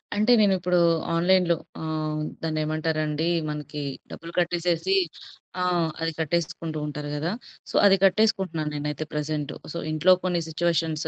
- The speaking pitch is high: No, medium, 160 Hz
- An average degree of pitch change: No, narrow, 2.3 semitones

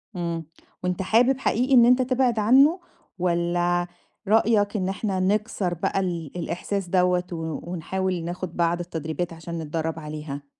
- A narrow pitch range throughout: No, average, 3.9 semitones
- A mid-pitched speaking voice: Yes, medium, 180 Hz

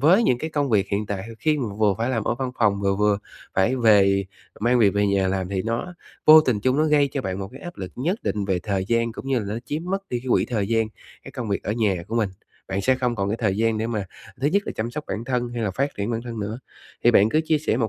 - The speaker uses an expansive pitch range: No, average, 4.6 semitones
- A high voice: No, low, 115 Hz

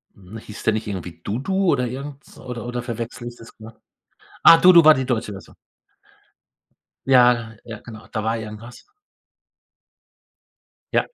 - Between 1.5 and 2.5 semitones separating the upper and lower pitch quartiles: No, average, 2.9 semitones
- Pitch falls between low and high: No, low, 120 Hz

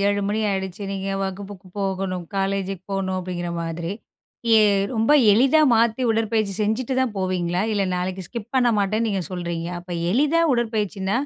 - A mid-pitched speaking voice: No, high, 195 Hz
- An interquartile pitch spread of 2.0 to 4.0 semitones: Yes, average, 3.0 semitones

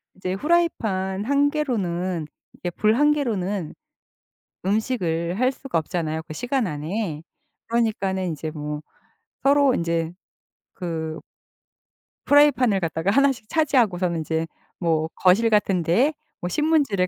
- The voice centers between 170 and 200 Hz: Yes, high, 190 Hz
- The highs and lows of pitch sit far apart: Yes, wide, 7.3 semitones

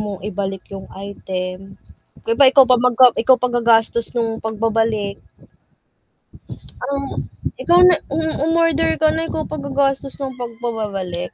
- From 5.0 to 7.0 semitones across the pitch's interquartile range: Yes, wide, 5.4 semitones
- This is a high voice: Yes, high, 240 Hz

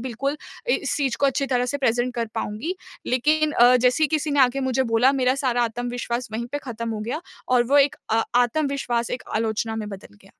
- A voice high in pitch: Yes, very high, 250 Hz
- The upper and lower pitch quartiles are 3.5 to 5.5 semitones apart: No, average, 2.9 semitones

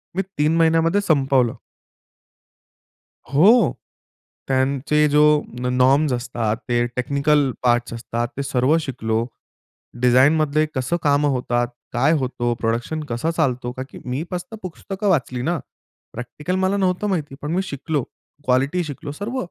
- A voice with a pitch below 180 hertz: Yes, medium, 140 Hz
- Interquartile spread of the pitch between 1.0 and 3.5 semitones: No, average, 4.4 semitones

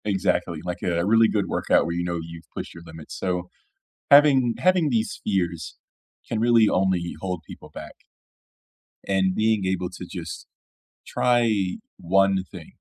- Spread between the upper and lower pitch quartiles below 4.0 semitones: No, average, 4.3 semitones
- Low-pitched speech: Yes, very low, 95 Hz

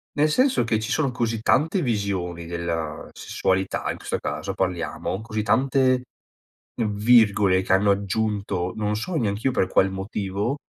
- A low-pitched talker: Yes, low, 105 Hz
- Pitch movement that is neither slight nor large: Yes, average, 4.1 semitones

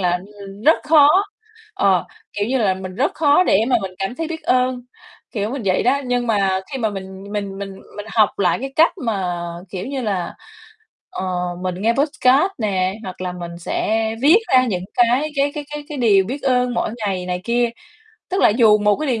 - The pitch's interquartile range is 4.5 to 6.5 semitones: Yes, wide, 5.5 semitones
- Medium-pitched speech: No, high, 220 Hz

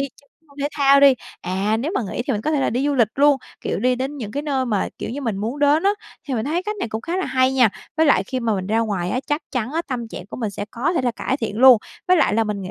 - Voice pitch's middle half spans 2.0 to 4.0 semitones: No, average, 4.6 semitones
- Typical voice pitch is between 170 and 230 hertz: No, very high, 255 Hz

